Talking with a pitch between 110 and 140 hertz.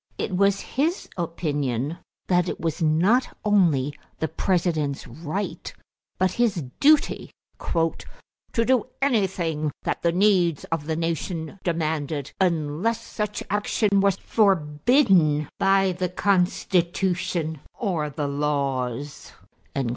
No: medium, 175 Hz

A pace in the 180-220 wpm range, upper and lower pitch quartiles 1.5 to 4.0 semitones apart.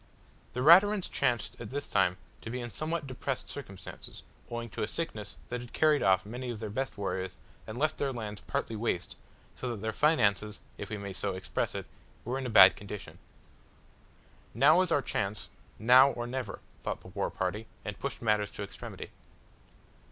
No: average, 185 wpm; average, 4.7 semitones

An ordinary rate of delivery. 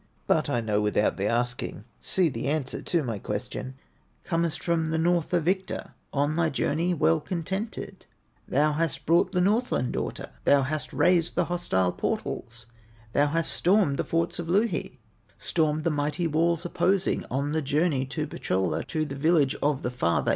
Yes: average, 170 wpm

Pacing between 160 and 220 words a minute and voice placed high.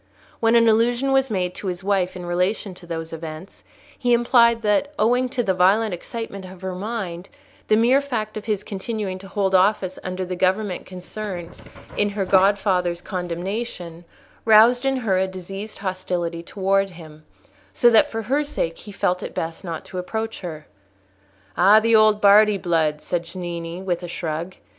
Yes: average, 175 wpm; high, 195 Hz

